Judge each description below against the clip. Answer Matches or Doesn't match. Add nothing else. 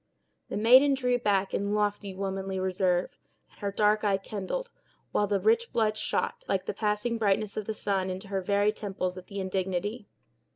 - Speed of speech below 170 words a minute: Doesn't match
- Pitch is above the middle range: Matches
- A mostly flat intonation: Matches